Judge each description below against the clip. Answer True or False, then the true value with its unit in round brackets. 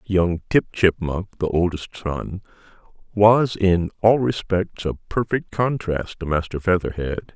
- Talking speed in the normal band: False (130 wpm)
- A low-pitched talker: True (95 Hz)